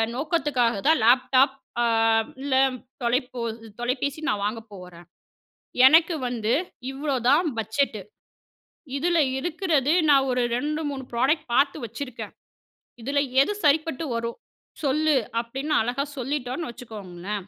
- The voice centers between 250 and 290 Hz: Yes, very high, 265 Hz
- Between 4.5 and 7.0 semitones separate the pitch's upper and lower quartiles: No, average, 4.0 semitones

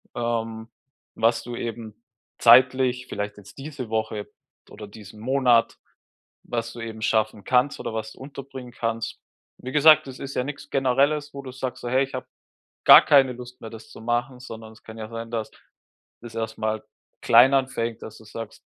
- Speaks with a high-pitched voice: No, low, 120 Hz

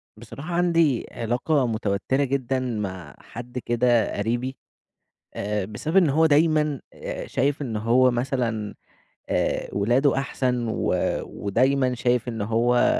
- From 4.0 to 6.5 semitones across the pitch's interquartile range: No, average, 3.5 semitones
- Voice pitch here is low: Yes, low, 125 Hz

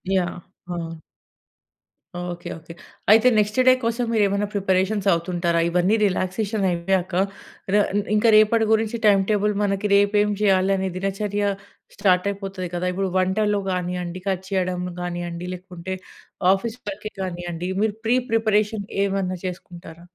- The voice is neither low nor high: No, high, 195 Hz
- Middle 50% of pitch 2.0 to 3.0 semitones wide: Yes, narrow, 2.6 semitones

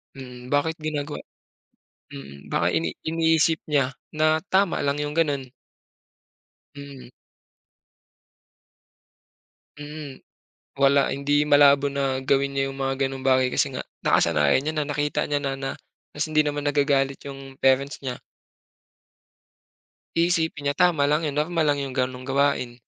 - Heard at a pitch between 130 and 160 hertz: Yes, medium, 140 Hz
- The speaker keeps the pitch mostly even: Yes, narrow, 1.7 semitones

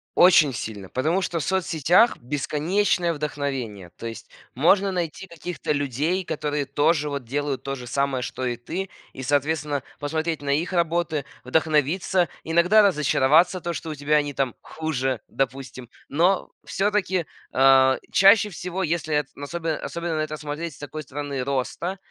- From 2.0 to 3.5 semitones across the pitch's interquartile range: No, average, 3.9 semitones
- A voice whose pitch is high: No, medium, 150 Hz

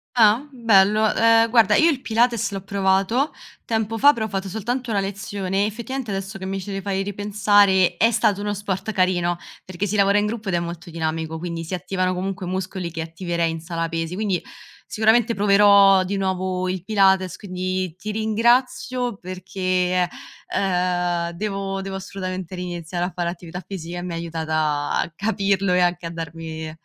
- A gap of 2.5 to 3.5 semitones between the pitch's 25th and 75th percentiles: Yes, average, 2.8 semitones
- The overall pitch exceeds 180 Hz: Yes, high, 190 Hz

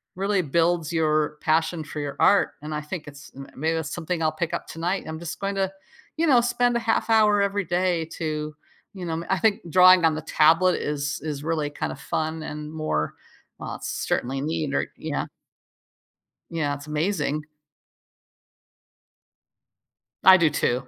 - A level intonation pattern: No, average, 3.5 semitones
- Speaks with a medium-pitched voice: Yes, medium, 160 Hz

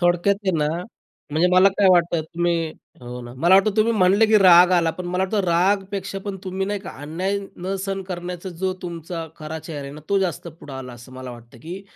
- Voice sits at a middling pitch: Yes, medium, 175 Hz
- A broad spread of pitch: No, average, 3.2 semitones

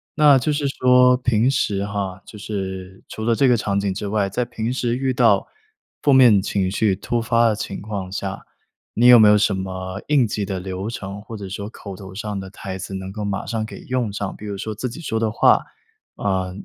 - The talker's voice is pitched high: No, low, 105 Hz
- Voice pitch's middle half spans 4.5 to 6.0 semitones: No, average, 3.4 semitones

